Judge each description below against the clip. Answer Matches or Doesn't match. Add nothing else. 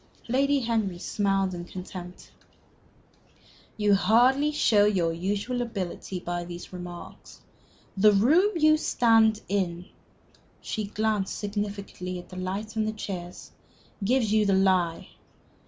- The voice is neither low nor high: Doesn't match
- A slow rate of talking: Matches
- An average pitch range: Matches